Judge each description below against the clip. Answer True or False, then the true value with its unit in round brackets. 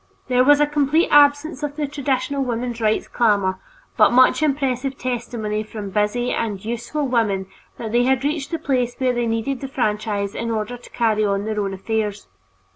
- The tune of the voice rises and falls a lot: False (4.2 semitones)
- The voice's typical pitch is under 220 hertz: False (240 Hz)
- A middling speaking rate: True (185 wpm)